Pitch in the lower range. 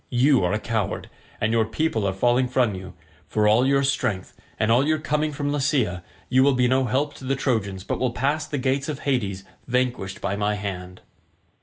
Yes: low, 125 Hz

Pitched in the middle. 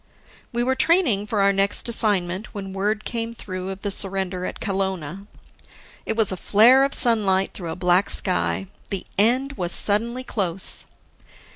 No: high, 200 Hz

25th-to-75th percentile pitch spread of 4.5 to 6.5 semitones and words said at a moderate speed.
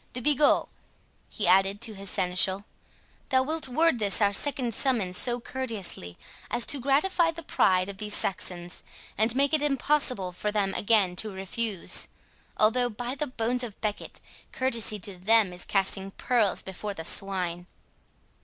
Yes: average, 4.9 semitones; average, 155 wpm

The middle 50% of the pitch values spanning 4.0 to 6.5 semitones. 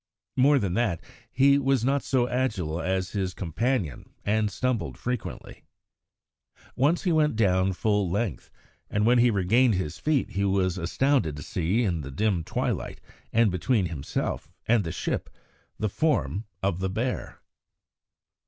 Yes: wide, 5.4 semitones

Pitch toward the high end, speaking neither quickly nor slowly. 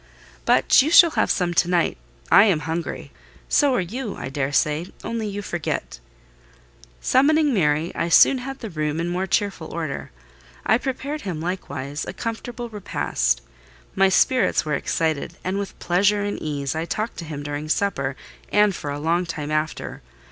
No: medium, 175 Hz; average, 170 wpm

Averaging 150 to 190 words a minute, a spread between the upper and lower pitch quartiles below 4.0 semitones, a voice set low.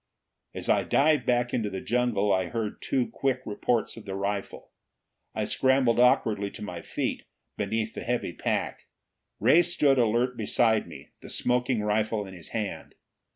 Yes: average, 160 wpm; average, 3.1 semitones; low, 115 Hz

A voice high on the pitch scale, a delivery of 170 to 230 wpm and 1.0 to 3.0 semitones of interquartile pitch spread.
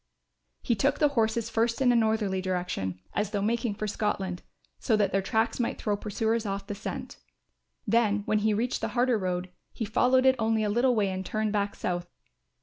Yes: high, 215 Hz; average, 200 wpm; narrow, 2.6 semitones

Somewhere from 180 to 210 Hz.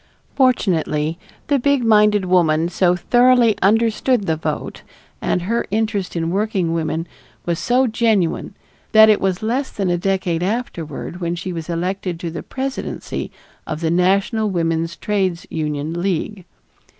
Yes: medium, 185 Hz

